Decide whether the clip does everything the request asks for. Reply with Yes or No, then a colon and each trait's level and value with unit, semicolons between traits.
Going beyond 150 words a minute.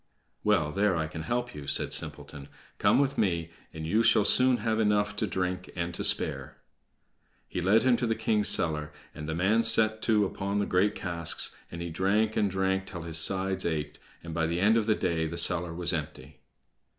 Yes: fast, 205 wpm